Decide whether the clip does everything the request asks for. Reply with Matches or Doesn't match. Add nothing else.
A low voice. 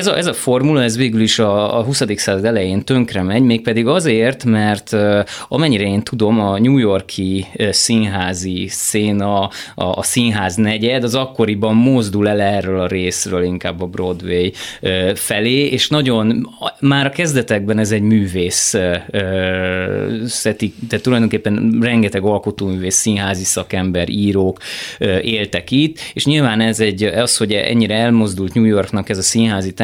Matches